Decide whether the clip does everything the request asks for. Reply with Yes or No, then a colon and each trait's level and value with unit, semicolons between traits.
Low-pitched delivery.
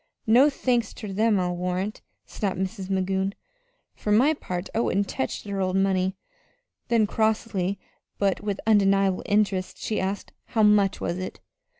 No: high, 200 Hz